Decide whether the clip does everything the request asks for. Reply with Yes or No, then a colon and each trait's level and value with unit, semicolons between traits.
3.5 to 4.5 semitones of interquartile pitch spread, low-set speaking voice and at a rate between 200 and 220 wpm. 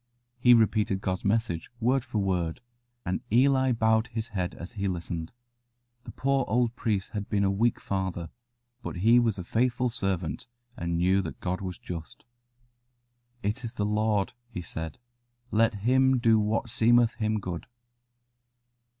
No: average, 4.1 semitones; low, 105 Hz; average, 155 wpm